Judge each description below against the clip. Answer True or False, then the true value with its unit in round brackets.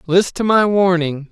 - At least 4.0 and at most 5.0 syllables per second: True (4.3 syllables/s)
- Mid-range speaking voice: True (180 Hz)